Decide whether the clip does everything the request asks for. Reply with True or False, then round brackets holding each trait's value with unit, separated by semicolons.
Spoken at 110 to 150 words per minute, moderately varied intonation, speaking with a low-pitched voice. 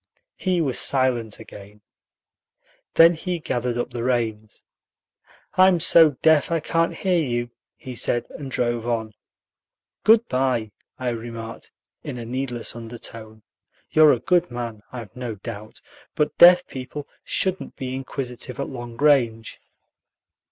True (135 wpm; 4.6 semitones; 125 Hz)